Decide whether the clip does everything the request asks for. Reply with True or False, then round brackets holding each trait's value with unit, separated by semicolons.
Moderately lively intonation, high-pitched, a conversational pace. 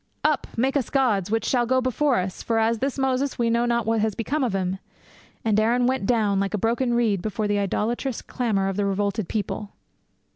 False (3.6 semitones; 225 Hz; 220 wpm)